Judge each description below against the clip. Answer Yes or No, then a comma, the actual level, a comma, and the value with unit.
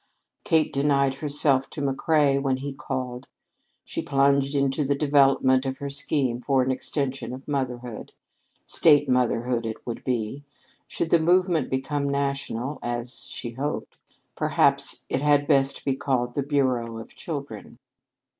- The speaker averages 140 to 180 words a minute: Yes, average, 145 wpm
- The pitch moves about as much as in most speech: No, narrow, 2.1 semitones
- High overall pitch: No, low, 135 Hz